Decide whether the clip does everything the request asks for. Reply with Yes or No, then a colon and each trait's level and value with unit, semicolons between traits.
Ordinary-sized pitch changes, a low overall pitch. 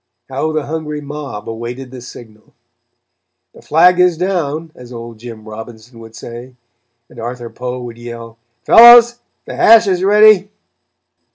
No: wide, 6.7 semitones; low, 125 Hz